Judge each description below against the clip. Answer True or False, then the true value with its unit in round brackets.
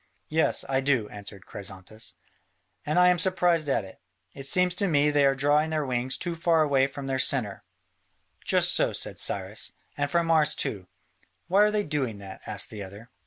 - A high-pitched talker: False (140 Hz)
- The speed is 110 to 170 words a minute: False (190 wpm)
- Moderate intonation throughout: False (6.1 semitones)